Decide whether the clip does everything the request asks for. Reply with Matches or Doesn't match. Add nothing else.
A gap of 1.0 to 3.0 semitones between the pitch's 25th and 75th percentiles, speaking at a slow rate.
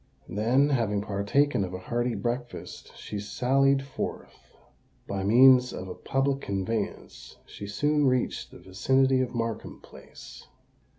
Doesn't match